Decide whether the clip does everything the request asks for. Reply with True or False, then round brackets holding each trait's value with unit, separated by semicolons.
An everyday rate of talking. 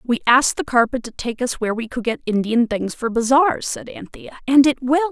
False (235 wpm)